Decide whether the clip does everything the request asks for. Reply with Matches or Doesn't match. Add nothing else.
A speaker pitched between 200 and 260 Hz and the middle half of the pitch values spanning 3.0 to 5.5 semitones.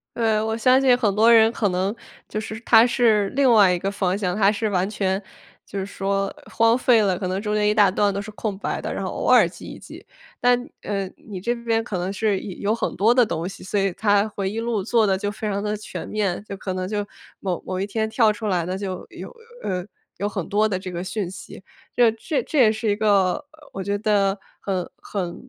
Doesn't match